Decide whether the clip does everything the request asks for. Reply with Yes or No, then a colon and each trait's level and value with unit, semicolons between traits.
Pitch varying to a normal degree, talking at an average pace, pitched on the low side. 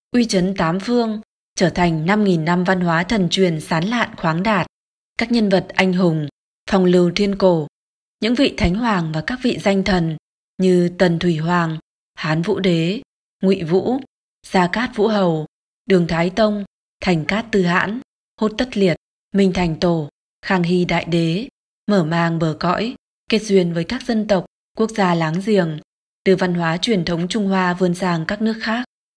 No: average, 3.6 semitones; average, 185 wpm; medium, 185 Hz